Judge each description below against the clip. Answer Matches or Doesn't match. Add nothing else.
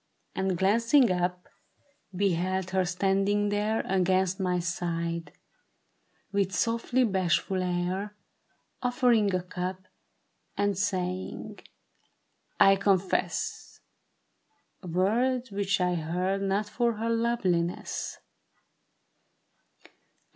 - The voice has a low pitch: Doesn't match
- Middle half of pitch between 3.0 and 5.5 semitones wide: Doesn't match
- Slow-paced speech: Matches